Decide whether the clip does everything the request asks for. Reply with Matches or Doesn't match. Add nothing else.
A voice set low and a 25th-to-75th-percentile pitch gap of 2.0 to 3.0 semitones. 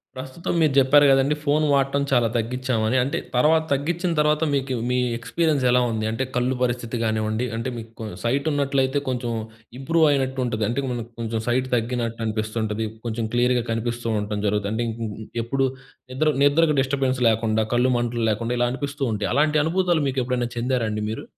Doesn't match